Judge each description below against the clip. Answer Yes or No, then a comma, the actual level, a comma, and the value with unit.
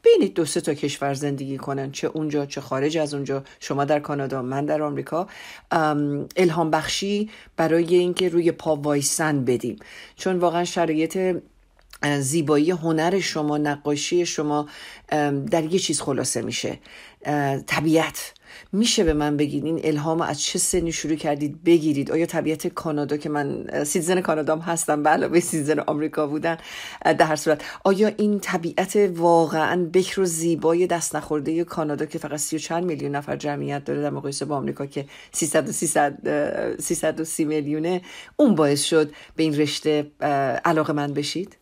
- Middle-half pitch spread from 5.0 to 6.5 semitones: No, narrow, 2.6 semitones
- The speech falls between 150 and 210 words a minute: Yes, fast, 155 wpm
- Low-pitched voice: No, medium, 155 Hz